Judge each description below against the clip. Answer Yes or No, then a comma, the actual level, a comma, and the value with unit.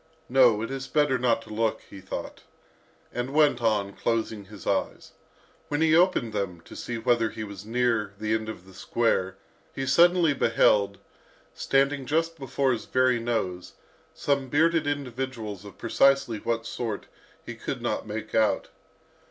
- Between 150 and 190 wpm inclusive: Yes, average, 160 wpm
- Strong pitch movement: No, average, 4.3 semitones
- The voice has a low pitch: Yes, low, 115 Hz